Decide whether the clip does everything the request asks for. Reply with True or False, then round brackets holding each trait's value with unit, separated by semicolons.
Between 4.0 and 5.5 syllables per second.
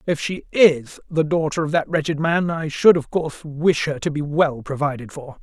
True (5.0 syllables/s)